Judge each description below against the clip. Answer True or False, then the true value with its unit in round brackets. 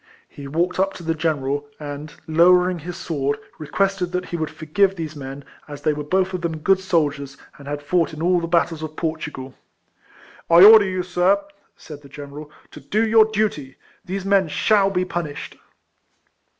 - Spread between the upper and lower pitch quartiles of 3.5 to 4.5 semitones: True (3.9 semitones)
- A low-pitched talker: False (165 Hz)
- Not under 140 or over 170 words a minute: False (190 wpm)